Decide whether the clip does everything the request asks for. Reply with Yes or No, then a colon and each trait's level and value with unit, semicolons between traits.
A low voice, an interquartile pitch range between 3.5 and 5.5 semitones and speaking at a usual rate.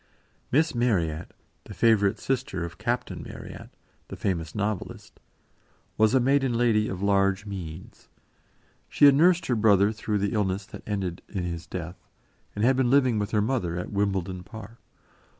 Yes: low, 105 Hz; average, 4.0 semitones; average, 160 wpm